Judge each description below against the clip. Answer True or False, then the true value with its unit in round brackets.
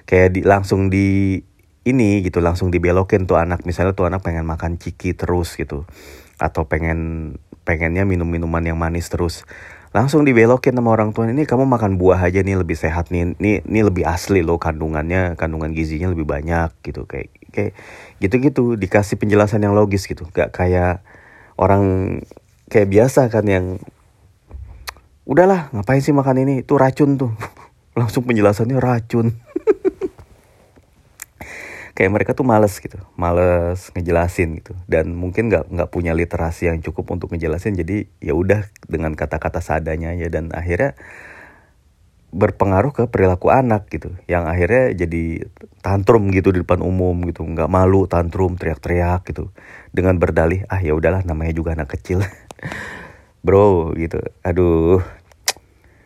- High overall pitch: False (90 Hz)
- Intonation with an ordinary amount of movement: True (3.6 semitones)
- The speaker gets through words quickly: True (145 wpm)